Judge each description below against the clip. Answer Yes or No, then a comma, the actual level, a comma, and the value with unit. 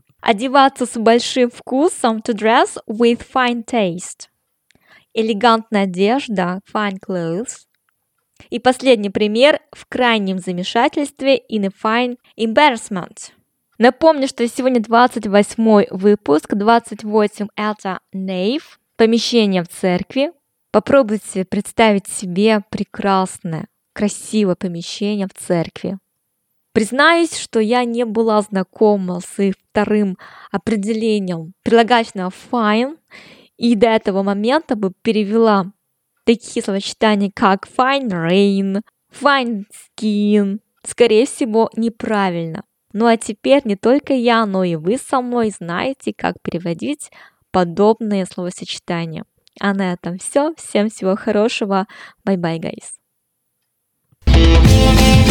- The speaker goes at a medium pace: No, slow, 105 wpm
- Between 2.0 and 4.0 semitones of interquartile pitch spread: Yes, average, 3.6 semitones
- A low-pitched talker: No, high, 215 Hz